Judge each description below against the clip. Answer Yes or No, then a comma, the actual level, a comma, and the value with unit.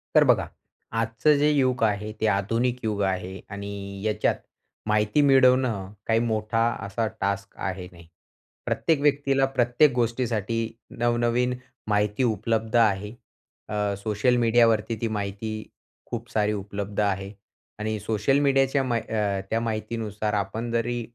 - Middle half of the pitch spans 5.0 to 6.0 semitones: No, average, 2.8 semitones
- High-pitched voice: No, low, 110 Hz